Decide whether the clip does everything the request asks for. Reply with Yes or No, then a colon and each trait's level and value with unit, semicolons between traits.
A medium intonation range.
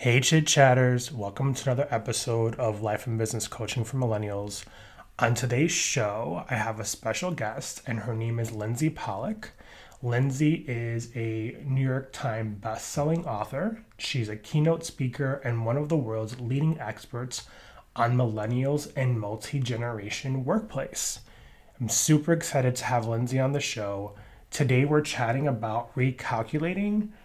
Yes: average, 4.1 semitones